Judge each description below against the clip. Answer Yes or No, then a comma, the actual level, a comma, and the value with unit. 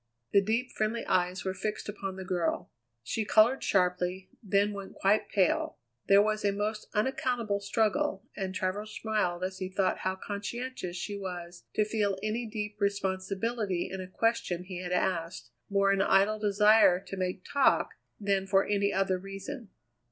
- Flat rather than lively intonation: Yes, narrow, 2.3 semitones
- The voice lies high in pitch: Yes, high, 200 Hz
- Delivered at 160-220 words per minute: Yes, average, 165 wpm